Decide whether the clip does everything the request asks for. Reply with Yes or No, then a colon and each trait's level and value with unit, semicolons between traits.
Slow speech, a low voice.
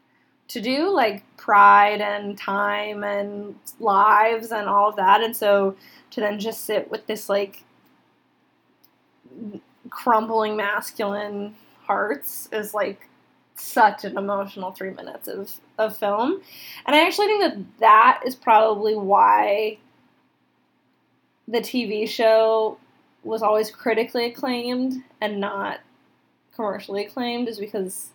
No: slow, 120 wpm; high, 215 Hz